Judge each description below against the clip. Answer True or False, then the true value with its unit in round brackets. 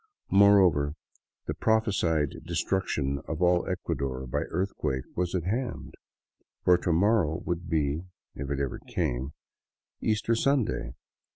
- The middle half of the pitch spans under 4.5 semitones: False (5.5 semitones)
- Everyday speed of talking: False (130 wpm)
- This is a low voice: True (85 Hz)